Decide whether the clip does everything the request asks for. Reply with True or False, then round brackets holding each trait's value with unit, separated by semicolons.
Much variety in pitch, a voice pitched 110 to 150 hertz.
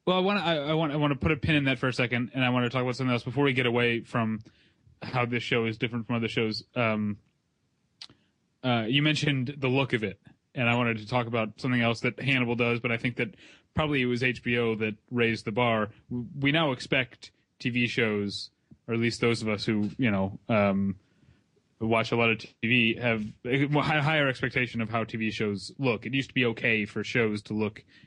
False (2.7 semitones; 120 Hz)